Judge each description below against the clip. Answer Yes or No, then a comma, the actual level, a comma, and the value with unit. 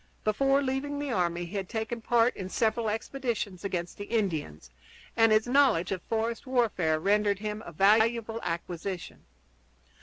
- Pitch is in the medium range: No, high, 215 Hz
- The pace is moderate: Yes, average, 150 wpm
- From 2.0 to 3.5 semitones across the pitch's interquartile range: No, average, 4.2 semitones